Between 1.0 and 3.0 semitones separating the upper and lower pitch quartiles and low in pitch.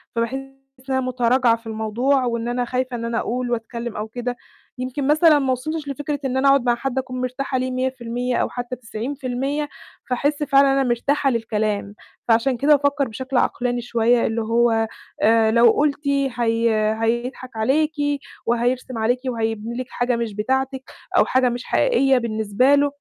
No: narrow, 2.6 semitones; very high, 250 Hz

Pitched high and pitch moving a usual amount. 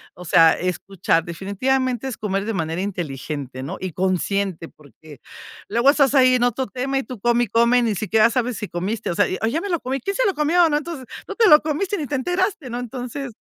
No: high, 235 Hz; wide, 6.4 semitones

